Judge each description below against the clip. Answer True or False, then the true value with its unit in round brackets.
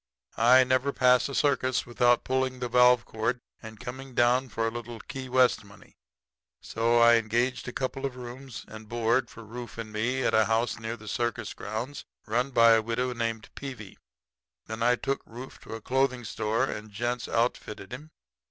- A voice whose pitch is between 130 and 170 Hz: False (120 Hz)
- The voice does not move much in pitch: True (2.2 semitones)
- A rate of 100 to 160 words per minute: False (190 wpm)